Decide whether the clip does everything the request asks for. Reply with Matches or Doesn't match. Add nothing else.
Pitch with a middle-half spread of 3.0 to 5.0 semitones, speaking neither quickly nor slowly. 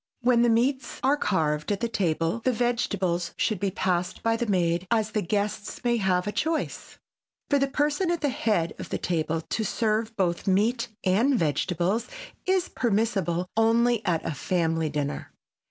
Doesn't match